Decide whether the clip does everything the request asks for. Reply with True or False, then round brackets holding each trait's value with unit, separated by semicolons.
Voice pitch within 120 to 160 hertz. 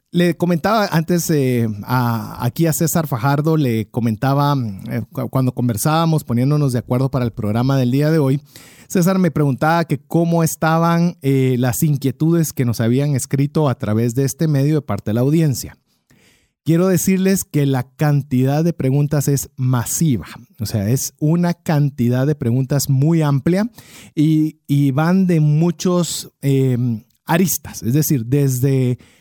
True (140 Hz)